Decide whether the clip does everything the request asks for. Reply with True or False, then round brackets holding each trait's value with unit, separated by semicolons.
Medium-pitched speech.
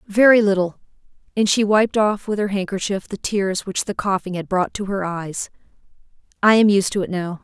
False (195 Hz)